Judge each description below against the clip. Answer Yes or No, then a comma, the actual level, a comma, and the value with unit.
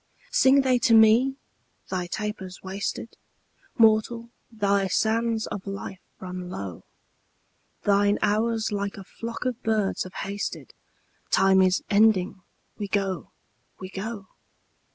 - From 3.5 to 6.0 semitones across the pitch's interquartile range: No, average, 2.7 semitones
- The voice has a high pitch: Yes, high, 205 Hz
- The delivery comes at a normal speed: No, slow, 120 wpm